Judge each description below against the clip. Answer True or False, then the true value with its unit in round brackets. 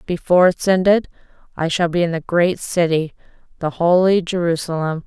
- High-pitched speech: False (175 Hz)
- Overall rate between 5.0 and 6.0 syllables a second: True (5.3 syllables/s)